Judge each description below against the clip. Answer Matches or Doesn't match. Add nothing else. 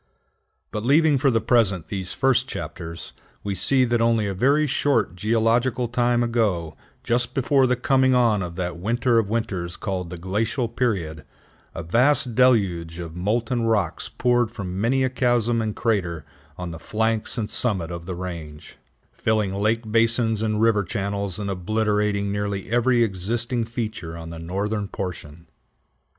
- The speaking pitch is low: Matches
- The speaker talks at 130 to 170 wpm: Matches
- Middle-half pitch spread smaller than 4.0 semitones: Doesn't match